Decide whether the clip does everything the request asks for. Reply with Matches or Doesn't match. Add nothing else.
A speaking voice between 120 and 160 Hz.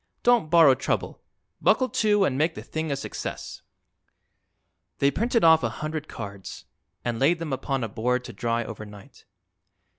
Matches